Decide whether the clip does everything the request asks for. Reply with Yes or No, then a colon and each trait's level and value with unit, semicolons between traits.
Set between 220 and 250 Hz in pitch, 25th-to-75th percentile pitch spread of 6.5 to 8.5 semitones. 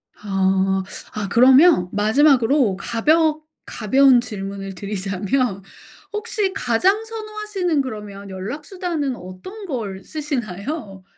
Yes: high, 240 Hz; wide, 8.0 semitones